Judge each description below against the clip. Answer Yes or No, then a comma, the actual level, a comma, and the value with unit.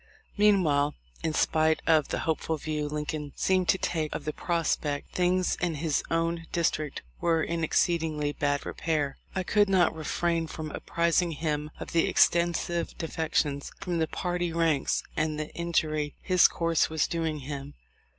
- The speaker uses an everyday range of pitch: No, narrow, 2.1 semitones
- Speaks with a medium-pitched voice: Yes, medium, 160 Hz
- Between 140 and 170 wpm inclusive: Yes, average, 155 wpm